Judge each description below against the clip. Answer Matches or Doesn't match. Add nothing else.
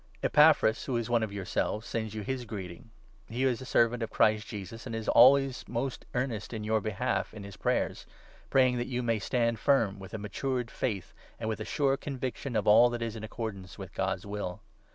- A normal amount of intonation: Matches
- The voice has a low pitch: Matches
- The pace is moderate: Doesn't match